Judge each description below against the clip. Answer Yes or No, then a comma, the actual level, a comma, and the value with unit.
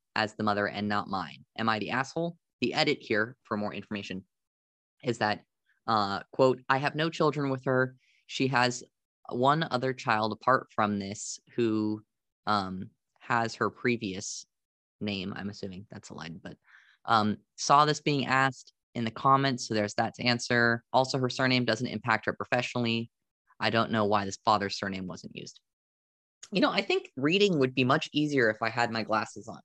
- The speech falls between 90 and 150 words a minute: No, average, 180 wpm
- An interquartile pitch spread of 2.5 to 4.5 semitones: Yes, average, 3.8 semitones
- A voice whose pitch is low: Yes, low, 115 Hz